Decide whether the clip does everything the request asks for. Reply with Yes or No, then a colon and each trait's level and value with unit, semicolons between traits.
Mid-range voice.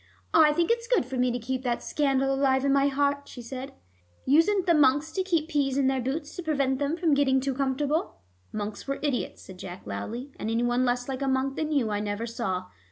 No: very high, 270 Hz